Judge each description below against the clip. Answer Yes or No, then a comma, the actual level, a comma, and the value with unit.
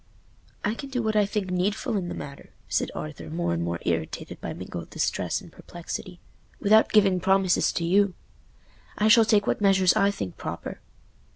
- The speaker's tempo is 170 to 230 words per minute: Yes, average, 180 wpm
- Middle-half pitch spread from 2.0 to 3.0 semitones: No, average, 3.9 semitones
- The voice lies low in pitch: No, high, 190 Hz